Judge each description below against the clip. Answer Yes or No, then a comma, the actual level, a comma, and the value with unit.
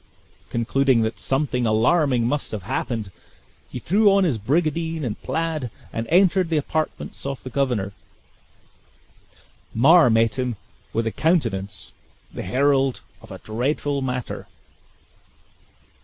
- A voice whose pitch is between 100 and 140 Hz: Yes, low, 135 Hz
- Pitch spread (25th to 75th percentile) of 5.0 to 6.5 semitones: Yes, average, 5.3 semitones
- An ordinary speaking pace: No, slow, 125 wpm